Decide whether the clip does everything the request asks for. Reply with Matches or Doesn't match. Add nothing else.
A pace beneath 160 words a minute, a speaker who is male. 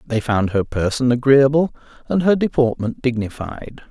Matches